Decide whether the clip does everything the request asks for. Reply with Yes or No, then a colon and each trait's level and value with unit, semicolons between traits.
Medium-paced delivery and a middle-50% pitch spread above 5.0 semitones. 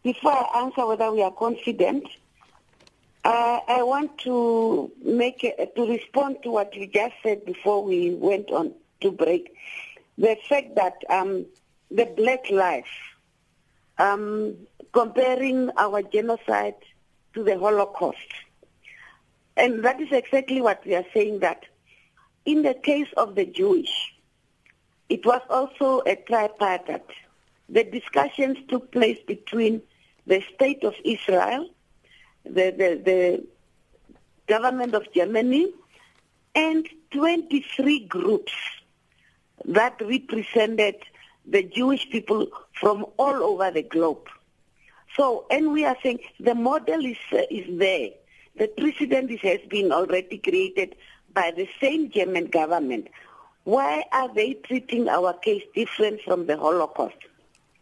No: slow, 125 wpm; wide, 5.6 semitones